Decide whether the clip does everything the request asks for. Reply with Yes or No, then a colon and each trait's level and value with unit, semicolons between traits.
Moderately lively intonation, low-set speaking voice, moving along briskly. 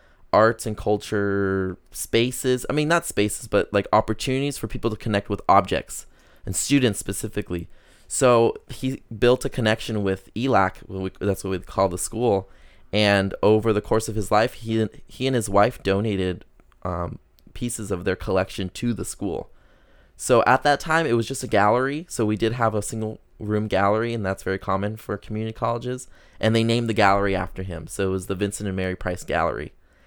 No: average, 3.3 semitones; low, 105 Hz; average, 190 wpm